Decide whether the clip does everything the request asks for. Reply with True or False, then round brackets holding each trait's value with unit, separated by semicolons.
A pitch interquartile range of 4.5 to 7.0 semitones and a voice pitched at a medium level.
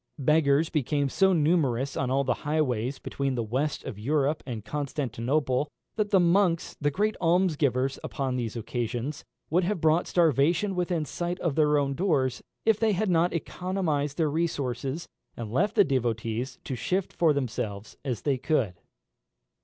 True (4.9 semitones; 145 Hz)